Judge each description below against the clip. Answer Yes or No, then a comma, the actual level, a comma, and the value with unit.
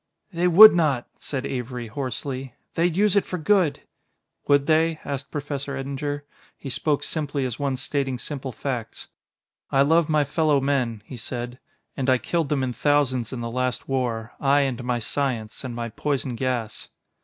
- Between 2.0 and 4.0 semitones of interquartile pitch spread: Yes, average, 2.8 semitones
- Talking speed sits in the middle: Yes, average, 170 wpm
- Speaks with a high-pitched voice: No, low, 135 Hz